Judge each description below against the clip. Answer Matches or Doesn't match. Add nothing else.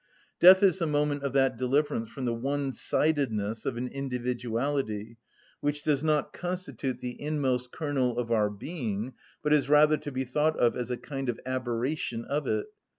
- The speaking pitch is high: Doesn't match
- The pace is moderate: Matches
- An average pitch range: Matches